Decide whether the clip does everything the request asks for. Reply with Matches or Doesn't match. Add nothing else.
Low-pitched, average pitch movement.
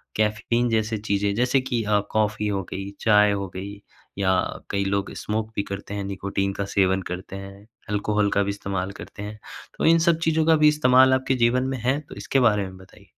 Matches